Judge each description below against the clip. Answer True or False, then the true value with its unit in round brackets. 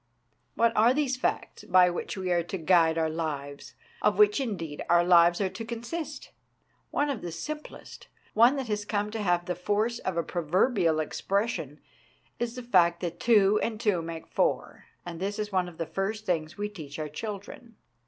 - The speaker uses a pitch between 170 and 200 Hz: True (190 Hz)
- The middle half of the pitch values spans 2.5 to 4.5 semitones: False (5.1 semitones)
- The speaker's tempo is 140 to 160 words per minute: False (190 wpm)